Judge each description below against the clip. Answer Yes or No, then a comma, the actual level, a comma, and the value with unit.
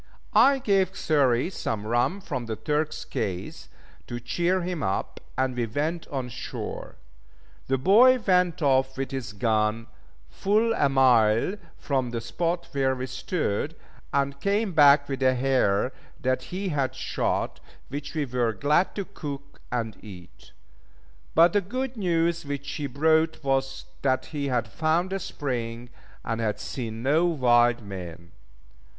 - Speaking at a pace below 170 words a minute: Yes, average, 150 wpm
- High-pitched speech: No, low, 135 Hz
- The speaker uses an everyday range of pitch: No, wide, 5.7 semitones